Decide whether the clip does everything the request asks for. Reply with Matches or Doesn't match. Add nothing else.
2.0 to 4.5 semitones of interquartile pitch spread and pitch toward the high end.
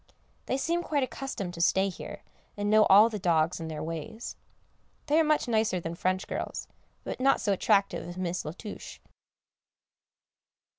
Doesn't match